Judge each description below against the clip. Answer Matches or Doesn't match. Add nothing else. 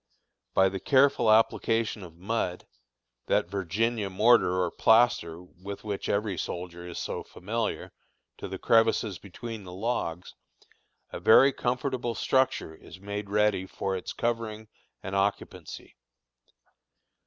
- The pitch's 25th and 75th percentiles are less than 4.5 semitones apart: Matches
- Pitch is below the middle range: Matches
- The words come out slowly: Matches